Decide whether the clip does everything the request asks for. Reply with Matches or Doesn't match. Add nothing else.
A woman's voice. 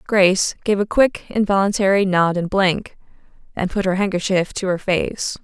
Matches